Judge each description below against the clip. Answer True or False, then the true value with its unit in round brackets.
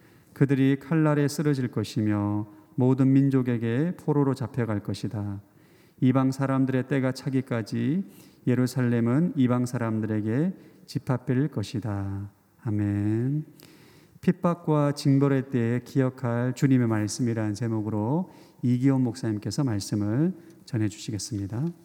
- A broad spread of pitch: False (4.9 semitones)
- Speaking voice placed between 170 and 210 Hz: False (130 Hz)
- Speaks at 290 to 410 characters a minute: False (275 characters per minute)